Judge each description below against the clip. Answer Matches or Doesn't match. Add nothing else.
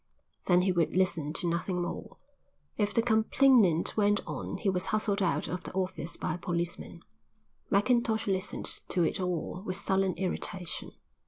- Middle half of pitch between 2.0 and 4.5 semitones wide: Matches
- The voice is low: Doesn't match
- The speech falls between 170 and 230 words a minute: Doesn't match